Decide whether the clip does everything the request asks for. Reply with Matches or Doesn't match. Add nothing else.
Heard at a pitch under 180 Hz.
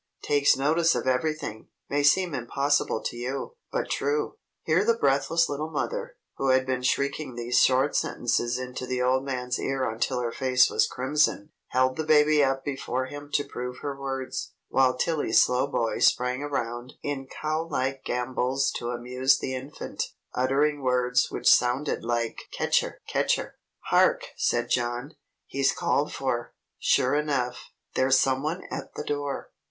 Matches